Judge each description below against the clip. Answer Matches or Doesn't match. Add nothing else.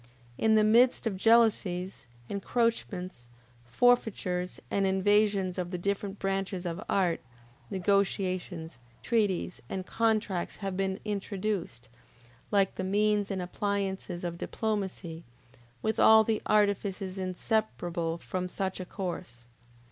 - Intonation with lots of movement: Doesn't match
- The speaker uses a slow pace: Matches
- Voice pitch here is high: Matches